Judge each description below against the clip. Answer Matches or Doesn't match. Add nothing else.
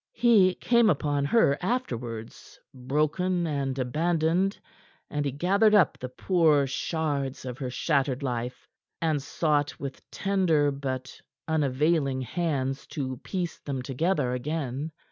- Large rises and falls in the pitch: Doesn't match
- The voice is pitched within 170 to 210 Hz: Doesn't match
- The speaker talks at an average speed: Doesn't match